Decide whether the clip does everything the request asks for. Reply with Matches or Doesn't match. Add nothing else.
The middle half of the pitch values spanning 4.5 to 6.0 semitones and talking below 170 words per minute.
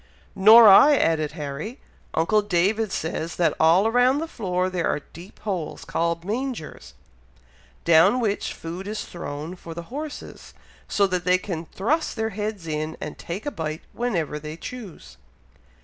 Matches